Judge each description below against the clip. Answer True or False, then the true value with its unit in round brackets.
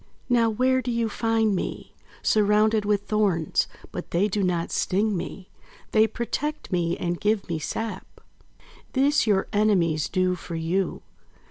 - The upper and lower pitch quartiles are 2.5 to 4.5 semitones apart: True (3.6 semitones)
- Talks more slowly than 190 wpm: True (145 wpm)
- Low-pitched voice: False (205 Hz)